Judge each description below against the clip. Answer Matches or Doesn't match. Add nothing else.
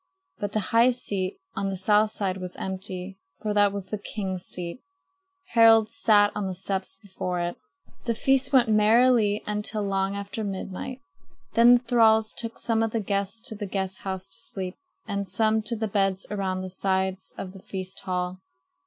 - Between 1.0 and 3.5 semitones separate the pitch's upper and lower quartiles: Matches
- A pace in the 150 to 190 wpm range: Matches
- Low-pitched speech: Doesn't match